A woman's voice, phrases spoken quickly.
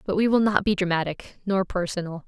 Yes: female; fast, 210 wpm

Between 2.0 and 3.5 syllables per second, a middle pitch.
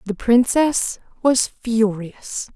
No: 2.8 syllables/s; high, 230 Hz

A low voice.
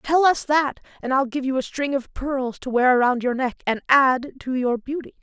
No: very high, 265 Hz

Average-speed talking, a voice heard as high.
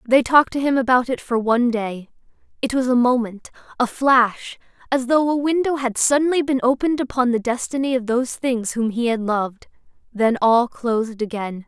Yes: average, 190 wpm; high, 245 Hz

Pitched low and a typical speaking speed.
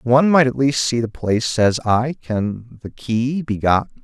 No: low, 120 Hz; fast, 210 wpm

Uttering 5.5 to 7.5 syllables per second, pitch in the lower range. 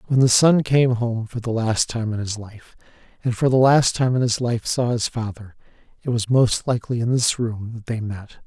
No: 5.0 syllables/s; low, 115 Hz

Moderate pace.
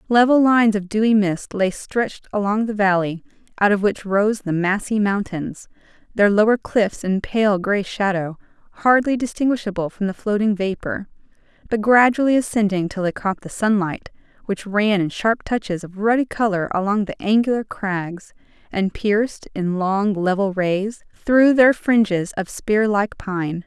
Yes: average, 155 wpm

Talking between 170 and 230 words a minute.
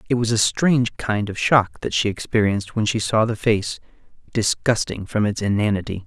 Yes: average, 190 wpm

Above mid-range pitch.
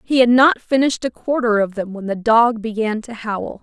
Yes: high, 230 Hz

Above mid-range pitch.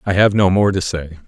No: very low, 95 Hz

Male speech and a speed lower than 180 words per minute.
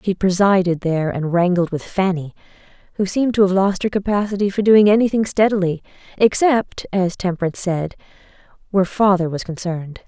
No: female; average, 155 wpm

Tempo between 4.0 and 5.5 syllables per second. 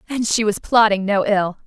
Yes: 5.0 syllables/s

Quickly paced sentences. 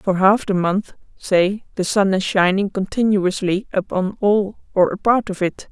No: average, 180 wpm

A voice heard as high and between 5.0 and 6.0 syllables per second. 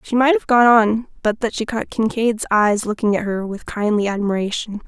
Yes: high, 220 Hz; 5.1 syllables/s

